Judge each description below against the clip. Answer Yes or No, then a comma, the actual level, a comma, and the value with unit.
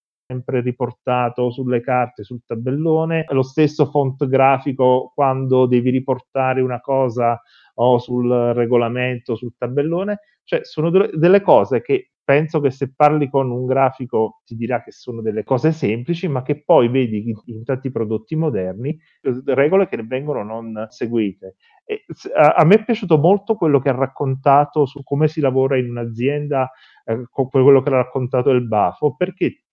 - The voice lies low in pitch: Yes, low, 130 Hz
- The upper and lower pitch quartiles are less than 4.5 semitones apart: Yes, average, 3.1 semitones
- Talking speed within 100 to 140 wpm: No, average, 160 wpm